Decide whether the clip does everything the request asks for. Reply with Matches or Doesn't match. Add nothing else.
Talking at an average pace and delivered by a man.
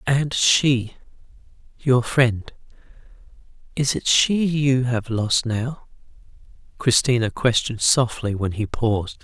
Doesn't match